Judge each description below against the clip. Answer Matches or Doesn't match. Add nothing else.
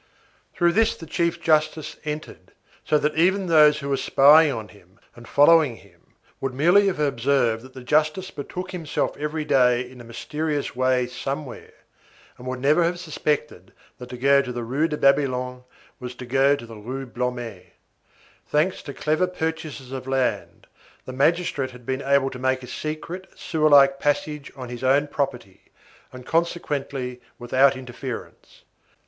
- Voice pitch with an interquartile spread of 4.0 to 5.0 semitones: Doesn't match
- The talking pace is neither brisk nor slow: Matches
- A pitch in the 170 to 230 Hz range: Doesn't match